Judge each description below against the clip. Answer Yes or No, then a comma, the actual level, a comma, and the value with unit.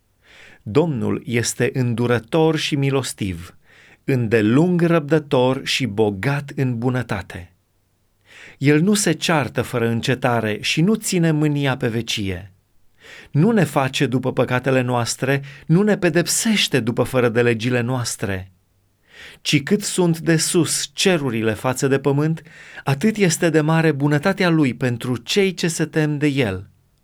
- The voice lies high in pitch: No, low, 135 Hz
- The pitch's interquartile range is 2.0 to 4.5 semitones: No, average, 5.2 semitones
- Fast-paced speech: No, average, 130 wpm